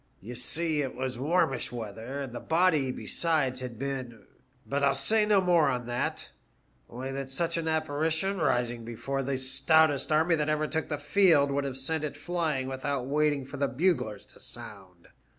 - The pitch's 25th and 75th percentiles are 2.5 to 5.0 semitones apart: Yes, average, 3.6 semitones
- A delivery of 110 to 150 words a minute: No, average, 185 wpm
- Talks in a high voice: No, medium, 140 Hz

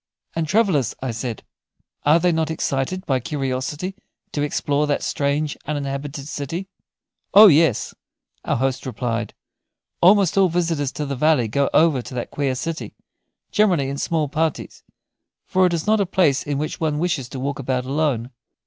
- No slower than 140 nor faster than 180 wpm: Yes, average, 165 wpm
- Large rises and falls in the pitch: No, average, 3.7 semitones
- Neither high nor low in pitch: Yes, medium, 145 Hz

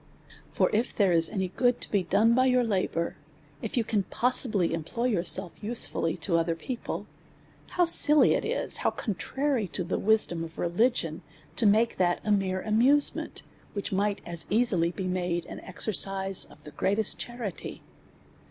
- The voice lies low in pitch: No, high, 200 Hz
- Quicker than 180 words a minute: No, average, 165 wpm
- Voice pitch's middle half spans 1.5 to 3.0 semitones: No, average, 4.8 semitones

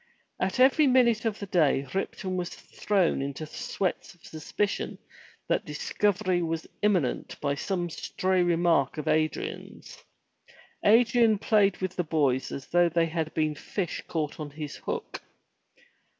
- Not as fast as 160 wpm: Yes, average, 140 wpm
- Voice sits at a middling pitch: Yes, medium, 175 Hz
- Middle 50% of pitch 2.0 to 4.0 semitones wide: No, average, 4.6 semitones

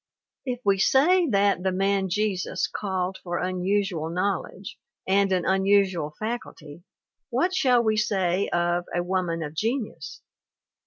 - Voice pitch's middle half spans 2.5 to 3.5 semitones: Yes, average, 2.9 semitones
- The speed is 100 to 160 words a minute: Yes, slow, 135 wpm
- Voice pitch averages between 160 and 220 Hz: Yes, high, 190 Hz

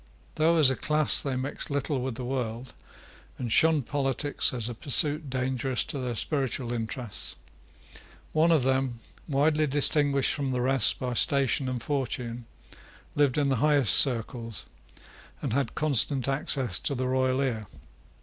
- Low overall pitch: Yes, low, 130 Hz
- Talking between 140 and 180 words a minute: Yes, average, 150 wpm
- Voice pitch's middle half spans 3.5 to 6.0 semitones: No, narrow, 2.6 semitones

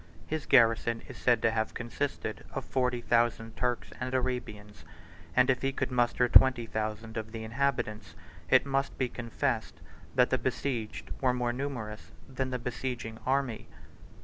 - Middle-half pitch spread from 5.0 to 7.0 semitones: No, narrow, 2.4 semitones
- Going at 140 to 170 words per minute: Yes, average, 155 wpm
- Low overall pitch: Yes, low, 120 Hz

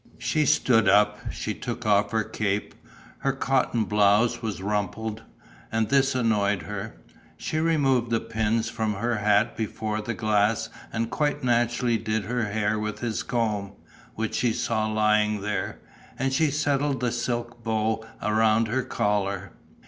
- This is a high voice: No, low, 110 Hz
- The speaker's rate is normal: Yes, average, 150 wpm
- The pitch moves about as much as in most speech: No, narrow, 2.3 semitones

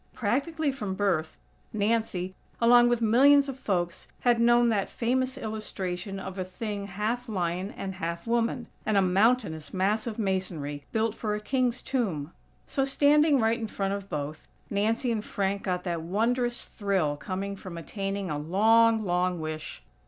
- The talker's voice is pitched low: No, high, 205 Hz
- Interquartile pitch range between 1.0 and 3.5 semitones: No, average, 4.2 semitones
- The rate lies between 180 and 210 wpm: No, average, 160 wpm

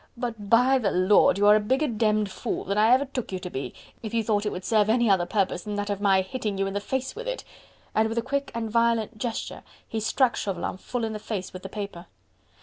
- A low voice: No, high, 215 Hz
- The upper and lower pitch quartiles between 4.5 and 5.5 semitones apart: No, average, 2.9 semitones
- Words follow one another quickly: Yes, fast, 255 wpm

